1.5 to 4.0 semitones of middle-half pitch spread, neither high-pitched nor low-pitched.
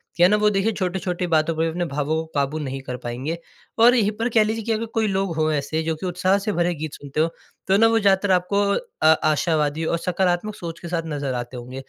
No: average, 4.4 semitones; medium, 170 Hz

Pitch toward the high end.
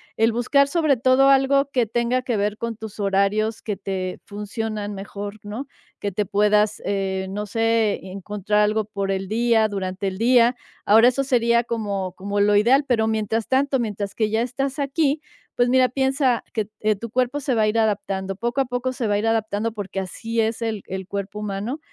Yes: high, 220 Hz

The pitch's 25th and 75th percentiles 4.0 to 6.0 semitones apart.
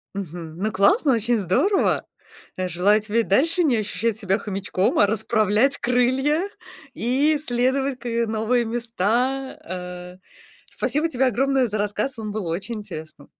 Yes: average, 4.7 semitones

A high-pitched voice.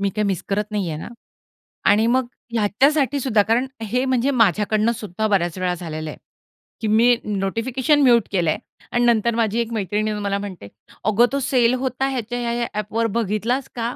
Yes: high, 225 Hz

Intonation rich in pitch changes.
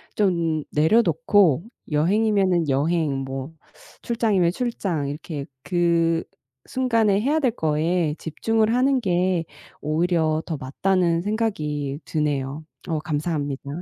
No: average, 5.0 semitones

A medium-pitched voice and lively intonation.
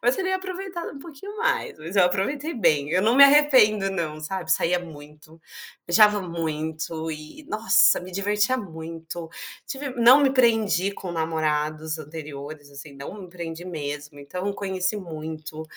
Yes: medium, 180 Hz; wide, 6.1 semitones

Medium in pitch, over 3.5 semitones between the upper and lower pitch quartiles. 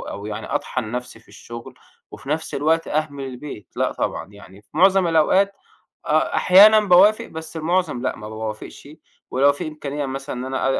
Yes: medium, 145 Hz; average, 4.9 semitones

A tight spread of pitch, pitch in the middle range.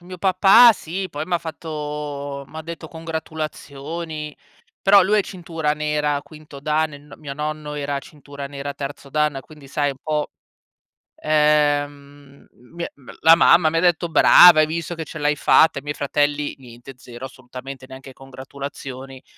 Yes: narrow, 2.3 semitones; medium, 150 Hz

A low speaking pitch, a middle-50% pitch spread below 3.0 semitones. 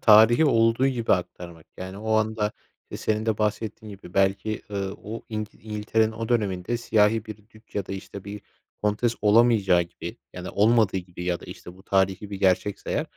Yes: low, 105 Hz; narrow, 2.5 semitones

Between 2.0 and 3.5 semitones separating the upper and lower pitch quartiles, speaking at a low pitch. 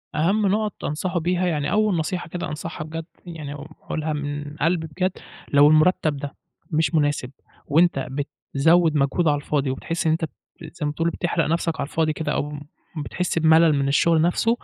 No: average, 2.7 semitones; medium, 160 Hz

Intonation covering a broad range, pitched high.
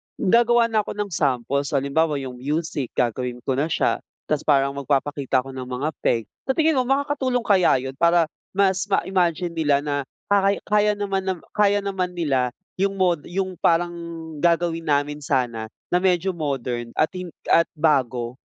No: wide, 5.9 semitones; medium, 165 Hz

